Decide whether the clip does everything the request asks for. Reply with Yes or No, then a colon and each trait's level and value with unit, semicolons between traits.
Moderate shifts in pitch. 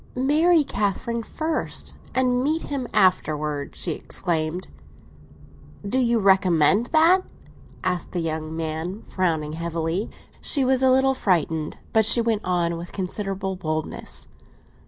No: wide, 7.4 semitones